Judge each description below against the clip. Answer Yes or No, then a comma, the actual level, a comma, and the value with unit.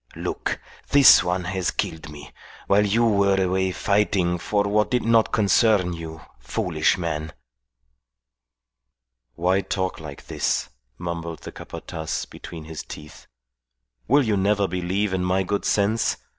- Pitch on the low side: Yes, very low, 95 Hz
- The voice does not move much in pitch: No, average, 3.4 semitones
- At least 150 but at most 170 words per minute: No, slow, 135 wpm